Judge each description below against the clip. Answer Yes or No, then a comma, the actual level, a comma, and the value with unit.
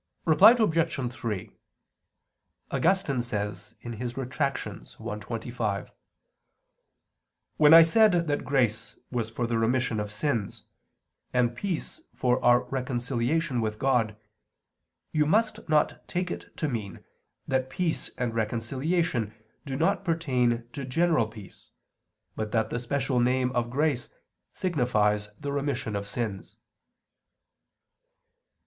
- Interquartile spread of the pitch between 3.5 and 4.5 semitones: No, average, 5.1 semitones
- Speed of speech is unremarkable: No, slow, 115 wpm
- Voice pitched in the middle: No, low, 125 Hz